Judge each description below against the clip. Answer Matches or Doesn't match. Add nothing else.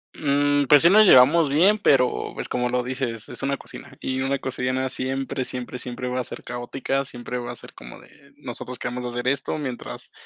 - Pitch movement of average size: Doesn't match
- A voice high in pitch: Doesn't match